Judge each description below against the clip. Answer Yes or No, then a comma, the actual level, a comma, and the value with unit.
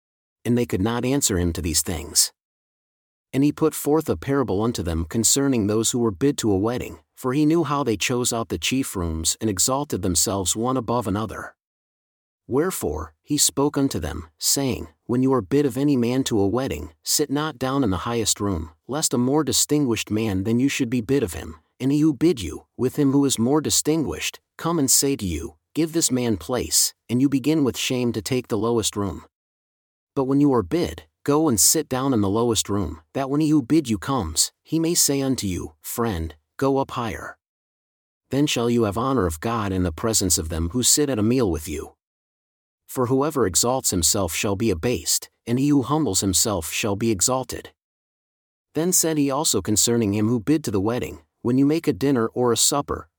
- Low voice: Yes, low, 115 Hz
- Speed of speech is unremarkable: No, fast, 210 wpm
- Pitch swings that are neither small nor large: No, wide, 6.6 semitones